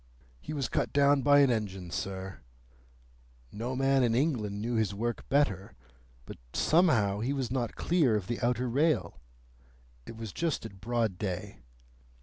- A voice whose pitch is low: Yes, low, 120 Hz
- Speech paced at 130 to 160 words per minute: Yes, average, 155 wpm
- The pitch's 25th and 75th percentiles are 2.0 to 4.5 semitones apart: No, average, 5.0 semitones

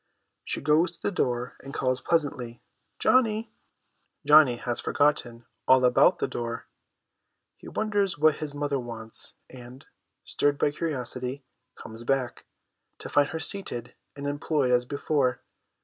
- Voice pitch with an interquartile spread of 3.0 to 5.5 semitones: Yes, average, 3.7 semitones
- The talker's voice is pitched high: No, medium, 140 Hz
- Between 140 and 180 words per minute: Yes, average, 145 wpm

